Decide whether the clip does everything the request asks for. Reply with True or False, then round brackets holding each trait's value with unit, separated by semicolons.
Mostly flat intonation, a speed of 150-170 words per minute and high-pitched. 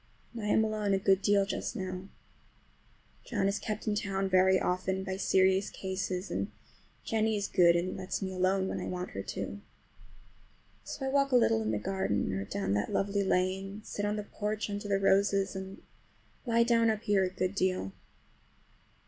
False (1.9 semitones; 190 wpm; 195 Hz)